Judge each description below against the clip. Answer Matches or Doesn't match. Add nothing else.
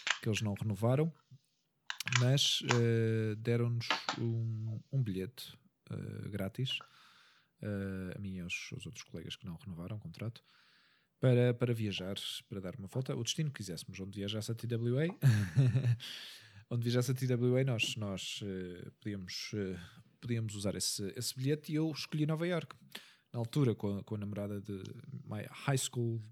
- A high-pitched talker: Doesn't match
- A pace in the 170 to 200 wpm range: Doesn't match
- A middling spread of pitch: Matches